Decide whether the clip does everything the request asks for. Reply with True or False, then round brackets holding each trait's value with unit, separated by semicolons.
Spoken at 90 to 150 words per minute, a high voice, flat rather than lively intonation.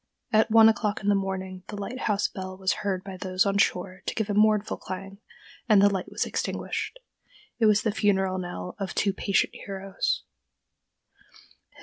False (175 wpm; 195 Hz; 1.9 semitones)